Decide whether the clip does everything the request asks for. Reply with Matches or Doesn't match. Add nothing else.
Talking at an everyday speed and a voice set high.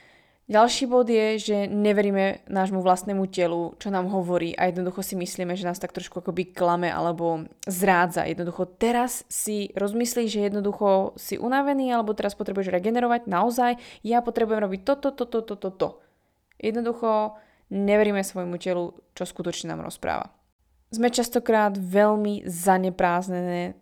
Matches